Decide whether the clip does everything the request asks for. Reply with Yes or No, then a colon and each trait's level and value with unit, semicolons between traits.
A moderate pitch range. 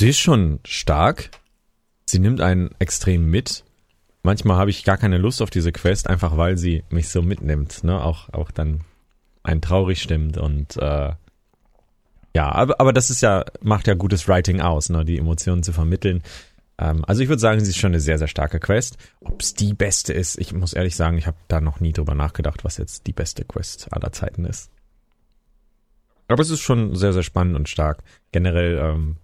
Yes: average, 3.5 semitones